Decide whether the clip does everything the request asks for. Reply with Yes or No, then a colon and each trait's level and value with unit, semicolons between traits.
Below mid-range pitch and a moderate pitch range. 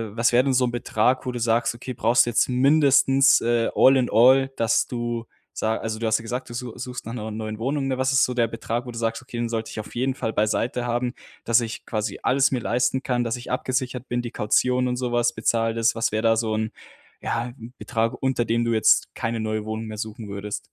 No: low, 120 Hz; narrow, 1.9 semitones